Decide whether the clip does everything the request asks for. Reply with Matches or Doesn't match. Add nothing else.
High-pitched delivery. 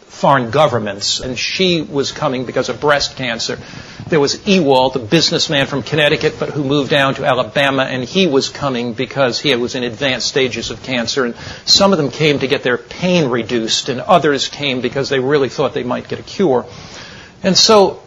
Doesn't match